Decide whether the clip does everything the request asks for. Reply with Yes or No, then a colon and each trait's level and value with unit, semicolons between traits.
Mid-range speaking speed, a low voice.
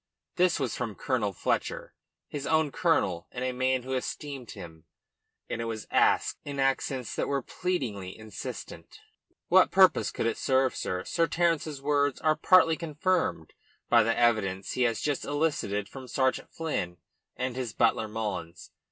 Yes: average, 160 wpm; low, 130 Hz